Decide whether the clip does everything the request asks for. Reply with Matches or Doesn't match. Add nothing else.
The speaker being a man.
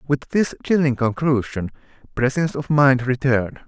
Matches